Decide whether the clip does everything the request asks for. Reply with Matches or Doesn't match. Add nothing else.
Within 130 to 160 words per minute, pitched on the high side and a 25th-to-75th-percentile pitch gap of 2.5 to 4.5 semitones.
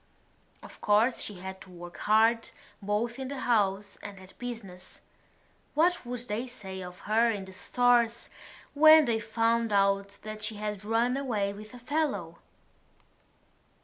Matches